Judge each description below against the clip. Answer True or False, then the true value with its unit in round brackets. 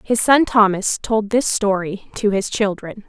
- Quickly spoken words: False (175 wpm)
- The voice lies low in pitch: False (210 Hz)